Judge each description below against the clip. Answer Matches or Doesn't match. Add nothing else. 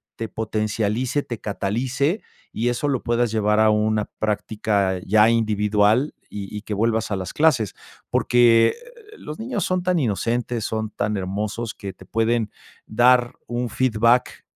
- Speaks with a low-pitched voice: Matches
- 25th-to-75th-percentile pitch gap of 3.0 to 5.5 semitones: Doesn't match